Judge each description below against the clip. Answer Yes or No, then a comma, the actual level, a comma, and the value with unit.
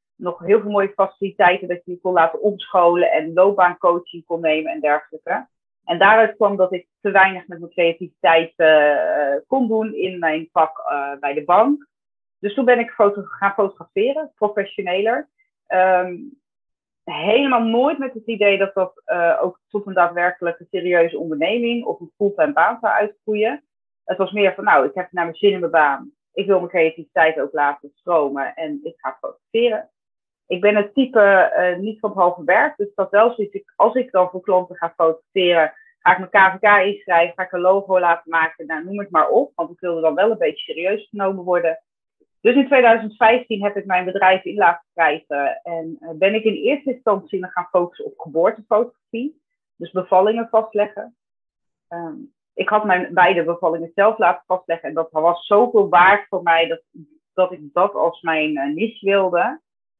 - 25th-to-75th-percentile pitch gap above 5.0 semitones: No, average, 4.2 semitones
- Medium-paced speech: Yes, average, 190 wpm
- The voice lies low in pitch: No, high, 190 Hz